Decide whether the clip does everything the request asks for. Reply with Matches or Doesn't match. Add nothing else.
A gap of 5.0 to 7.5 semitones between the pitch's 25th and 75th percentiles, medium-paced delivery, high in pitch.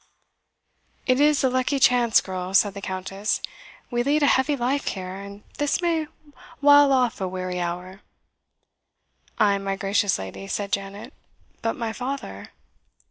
Matches